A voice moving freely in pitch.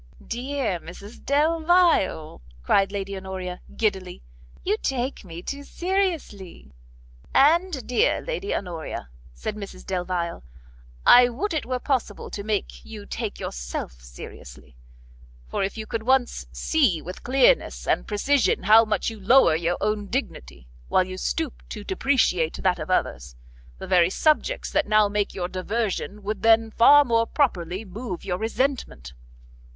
Yes: wide, 6.5 semitones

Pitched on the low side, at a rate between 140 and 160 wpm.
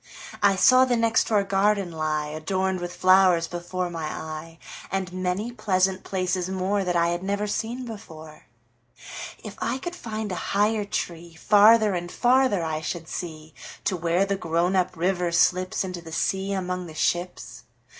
No: medium, 185 Hz; average, 145 wpm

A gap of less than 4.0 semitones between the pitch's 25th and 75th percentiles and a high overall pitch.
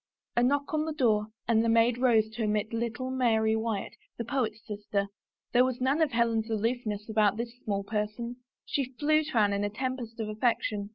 Yes: average, 2.9 semitones; high, 230 Hz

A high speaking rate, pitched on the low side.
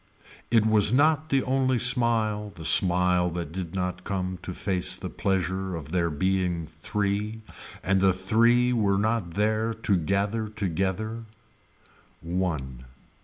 No: slow, 135 wpm; very low, 95 Hz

